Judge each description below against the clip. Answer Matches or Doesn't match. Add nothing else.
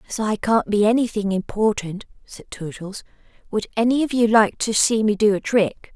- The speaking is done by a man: Doesn't match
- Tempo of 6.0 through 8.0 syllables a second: Doesn't match